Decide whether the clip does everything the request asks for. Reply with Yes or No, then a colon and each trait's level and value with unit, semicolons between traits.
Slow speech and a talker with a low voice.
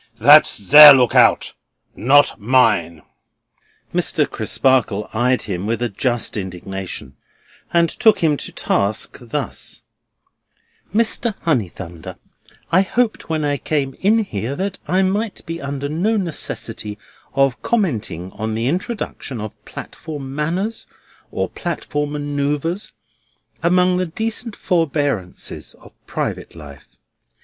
No: slow, 120 wpm; medium, 145 Hz